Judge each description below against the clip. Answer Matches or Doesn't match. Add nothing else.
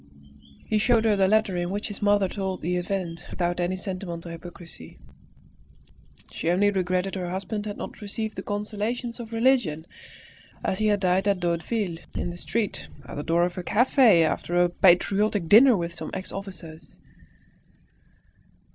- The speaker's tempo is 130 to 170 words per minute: Matches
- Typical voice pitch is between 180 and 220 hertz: Matches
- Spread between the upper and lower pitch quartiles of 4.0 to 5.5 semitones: Doesn't match